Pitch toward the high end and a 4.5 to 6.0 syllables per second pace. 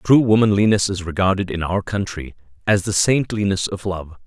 No: very low, 95 Hz; 5.3 syllables/s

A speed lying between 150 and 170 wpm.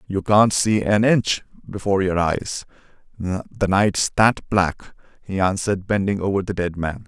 Yes: average, 155 wpm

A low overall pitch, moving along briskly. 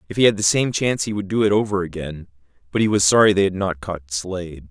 Yes: very low, 95 Hz; fast, 270 wpm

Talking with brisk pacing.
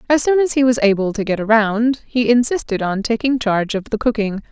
Yes: fast, 225 wpm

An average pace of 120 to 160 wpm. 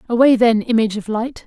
No: fast, 205 wpm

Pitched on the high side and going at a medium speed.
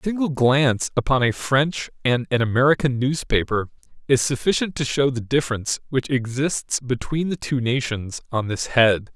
No: low, 130 Hz; average, 165 wpm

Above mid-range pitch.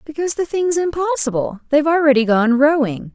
Yes: very high, 285 Hz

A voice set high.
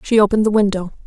Yes: high, 205 Hz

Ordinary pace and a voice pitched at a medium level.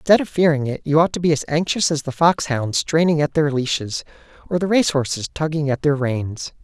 No: fast, 235 wpm; medium, 150 Hz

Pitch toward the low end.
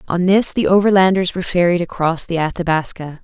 No: medium, 175 Hz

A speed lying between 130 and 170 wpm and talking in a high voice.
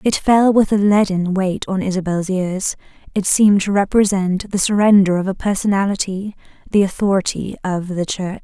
Yes: average, 165 wpm; high, 195 Hz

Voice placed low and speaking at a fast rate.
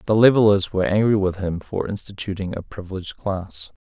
No: very low, 95 Hz; average, 175 wpm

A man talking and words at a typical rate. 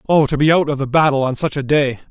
No: male; fast, 315 wpm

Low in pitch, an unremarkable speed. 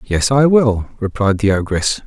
Yes: low, 110 Hz; average, 175 wpm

